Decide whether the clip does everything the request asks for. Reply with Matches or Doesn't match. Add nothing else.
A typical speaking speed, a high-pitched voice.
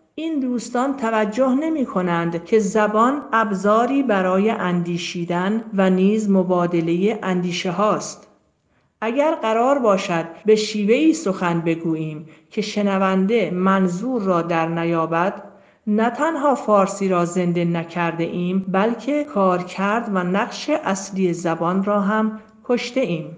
Matches